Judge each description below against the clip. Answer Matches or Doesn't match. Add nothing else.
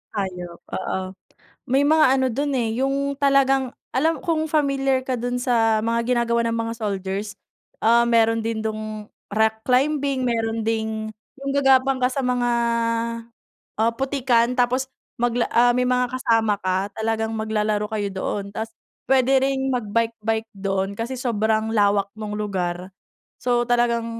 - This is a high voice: Matches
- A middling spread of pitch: Matches